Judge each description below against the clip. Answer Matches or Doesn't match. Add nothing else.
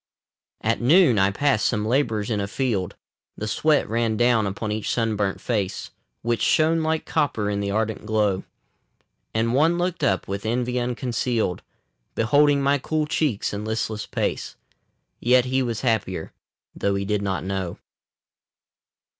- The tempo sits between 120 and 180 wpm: Matches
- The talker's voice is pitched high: Doesn't match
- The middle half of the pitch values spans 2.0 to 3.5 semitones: Doesn't match